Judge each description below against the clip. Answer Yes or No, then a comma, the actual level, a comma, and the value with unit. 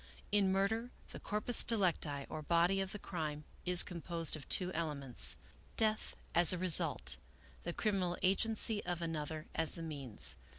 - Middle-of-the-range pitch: Yes, medium, 175 Hz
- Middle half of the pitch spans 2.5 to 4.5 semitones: Yes, average, 3.9 semitones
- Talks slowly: No, average, 165 wpm